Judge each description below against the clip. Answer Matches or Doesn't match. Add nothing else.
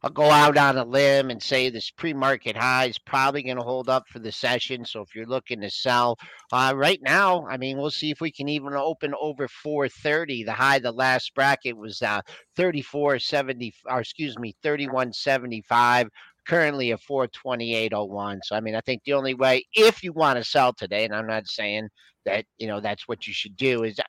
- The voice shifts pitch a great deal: Doesn't match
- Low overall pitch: Matches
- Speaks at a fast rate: Matches